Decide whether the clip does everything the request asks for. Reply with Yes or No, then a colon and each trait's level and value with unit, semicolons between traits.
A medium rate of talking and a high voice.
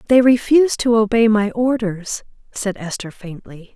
Yes: average, 145 wpm; high, 220 Hz